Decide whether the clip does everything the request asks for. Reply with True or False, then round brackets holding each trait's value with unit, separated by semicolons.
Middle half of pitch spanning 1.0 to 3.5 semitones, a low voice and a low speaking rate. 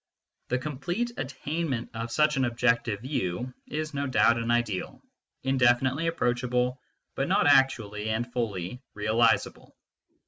True (2.9 semitones; 125 Hz; 125 wpm)